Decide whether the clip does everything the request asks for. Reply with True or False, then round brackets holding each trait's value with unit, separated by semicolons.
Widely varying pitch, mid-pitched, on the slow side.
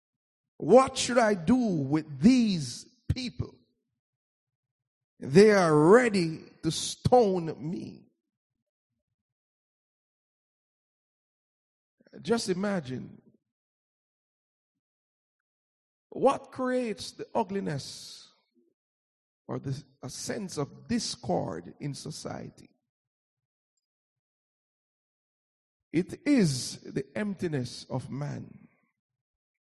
True (8.5 semitones; 155 Hz; 65 wpm)